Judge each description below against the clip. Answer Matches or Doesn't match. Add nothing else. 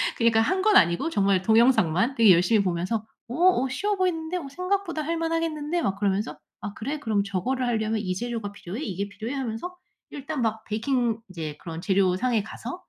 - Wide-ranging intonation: Matches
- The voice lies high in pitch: Matches